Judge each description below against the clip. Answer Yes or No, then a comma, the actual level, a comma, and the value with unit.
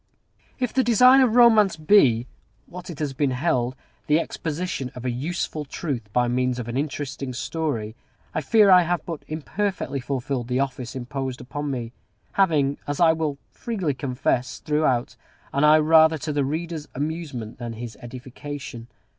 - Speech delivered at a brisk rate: No, average, 165 wpm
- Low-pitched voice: No, medium, 145 Hz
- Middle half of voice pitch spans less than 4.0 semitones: No, average, 4.5 semitones